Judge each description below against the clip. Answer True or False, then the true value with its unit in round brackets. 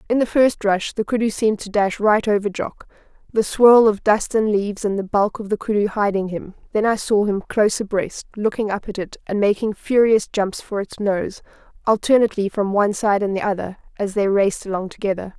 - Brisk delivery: True (210 wpm)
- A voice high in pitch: True (205 Hz)